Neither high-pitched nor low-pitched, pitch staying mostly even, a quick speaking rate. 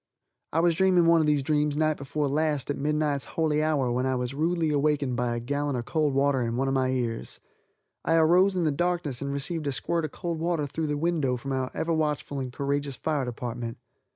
No: medium, 145 Hz; average, 3.2 semitones; fast, 225 wpm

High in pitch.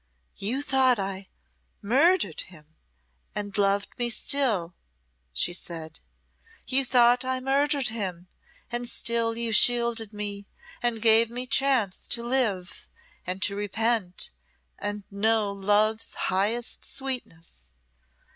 Yes: high, 220 Hz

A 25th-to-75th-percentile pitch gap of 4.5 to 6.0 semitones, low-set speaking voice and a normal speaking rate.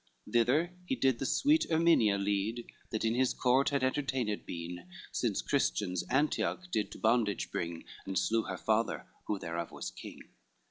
Yes: average, 5.1 semitones; low, 115 Hz; average, 165 wpm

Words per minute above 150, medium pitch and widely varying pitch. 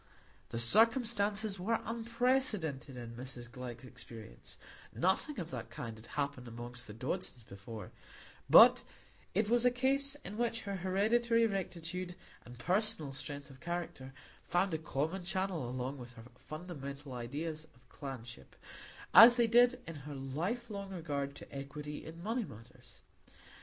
No: average, 140 wpm; medium, 160 Hz; wide, 8.6 semitones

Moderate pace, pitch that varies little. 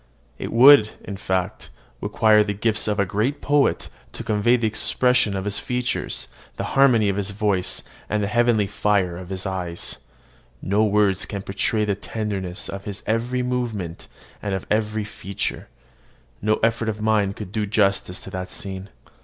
Yes: average, 170 wpm; narrow, 2.2 semitones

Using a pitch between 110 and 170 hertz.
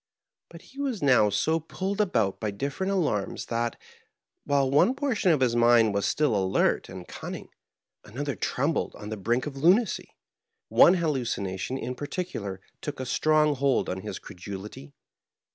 Yes: low, 135 Hz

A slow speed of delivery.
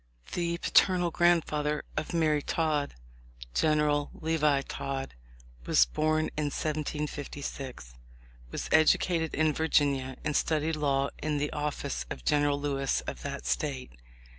Yes: slow, 125 wpm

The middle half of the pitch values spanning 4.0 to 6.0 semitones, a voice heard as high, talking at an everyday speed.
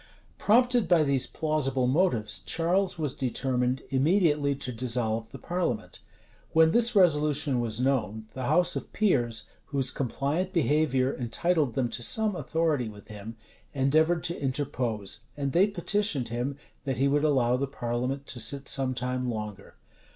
No: average, 4.7 semitones; low, 135 Hz; average, 150 wpm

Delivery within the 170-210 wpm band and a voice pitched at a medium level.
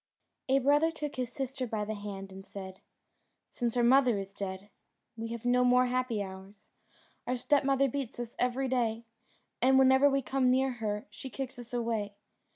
No: average, 175 wpm; high, 245 Hz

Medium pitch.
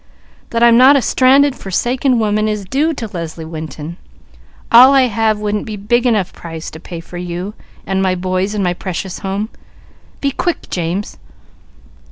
No: high, 205 Hz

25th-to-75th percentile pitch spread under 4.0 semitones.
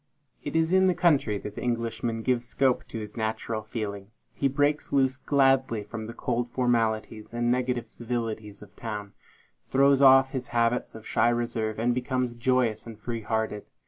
Yes: average, 2.8 semitones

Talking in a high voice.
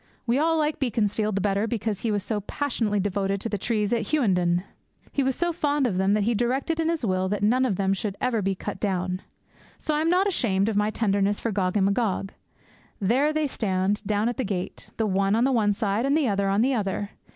Yes: high, 210 Hz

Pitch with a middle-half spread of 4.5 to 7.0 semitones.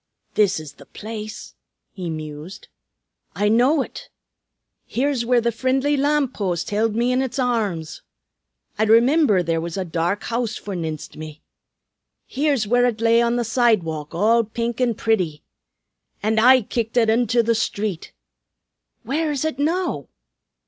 Yes: average, 4.9 semitones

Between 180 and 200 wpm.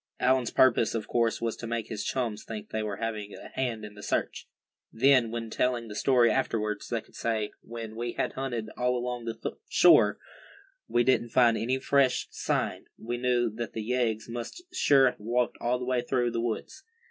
Yes: average, 195 wpm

